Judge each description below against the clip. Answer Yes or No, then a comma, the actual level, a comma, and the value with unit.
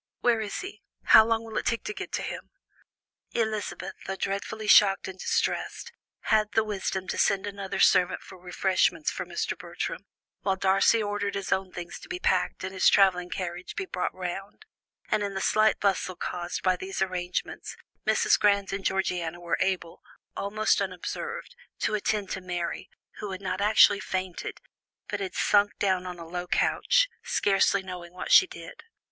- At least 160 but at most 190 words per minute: Yes, average, 175 wpm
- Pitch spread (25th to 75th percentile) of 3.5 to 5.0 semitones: No, narrow, 2.5 semitones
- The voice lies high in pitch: Yes, high, 195 Hz